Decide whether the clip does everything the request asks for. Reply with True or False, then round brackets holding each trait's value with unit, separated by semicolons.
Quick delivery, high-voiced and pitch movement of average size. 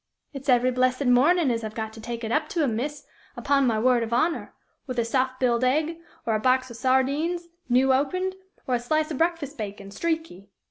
True (215 wpm; 255 Hz; 4.2 semitones)